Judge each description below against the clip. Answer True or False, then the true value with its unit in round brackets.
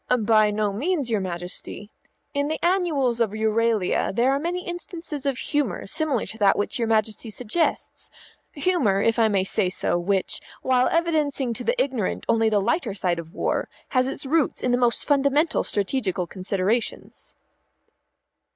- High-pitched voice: True (235 Hz)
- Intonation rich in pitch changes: True (5.8 semitones)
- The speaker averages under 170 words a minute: True (160 wpm)